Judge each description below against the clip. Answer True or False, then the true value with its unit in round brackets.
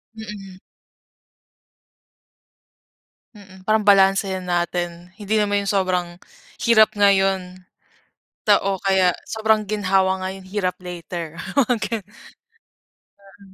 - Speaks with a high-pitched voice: True (195 Hz)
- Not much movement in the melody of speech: True (2.1 semitones)